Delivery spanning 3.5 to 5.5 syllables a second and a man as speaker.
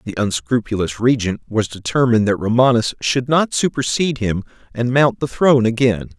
Yes: 5.4 syllables/s; male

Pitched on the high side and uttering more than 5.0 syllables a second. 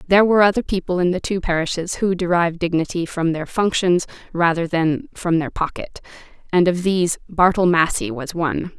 No: medium, 175 Hz; 5.5 syllables/s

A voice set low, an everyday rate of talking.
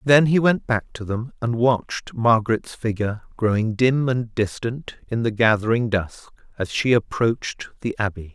Yes: low, 115 Hz; average, 165 wpm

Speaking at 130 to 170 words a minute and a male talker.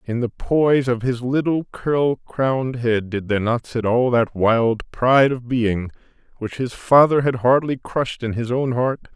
No: average, 190 wpm; male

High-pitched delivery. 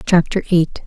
No: medium, 175 Hz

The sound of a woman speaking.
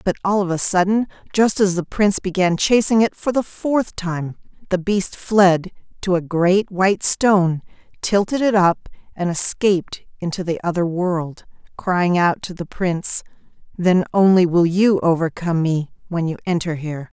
Yes: female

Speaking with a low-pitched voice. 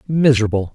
Yes: low, 125 Hz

